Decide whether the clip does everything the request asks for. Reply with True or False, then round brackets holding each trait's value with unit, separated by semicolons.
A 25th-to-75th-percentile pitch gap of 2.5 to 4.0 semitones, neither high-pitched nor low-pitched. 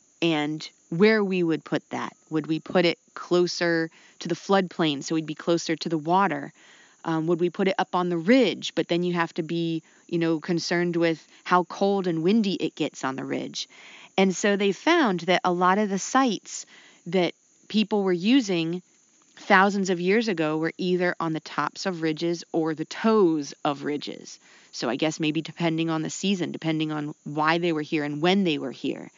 True (2.8 semitones; 170 Hz)